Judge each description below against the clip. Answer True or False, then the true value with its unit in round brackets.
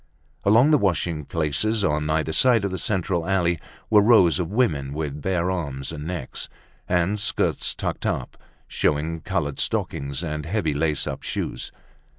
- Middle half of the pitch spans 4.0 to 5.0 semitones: True (4.4 semitones)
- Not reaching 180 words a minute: True (160 wpm)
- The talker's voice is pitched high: False (85 Hz)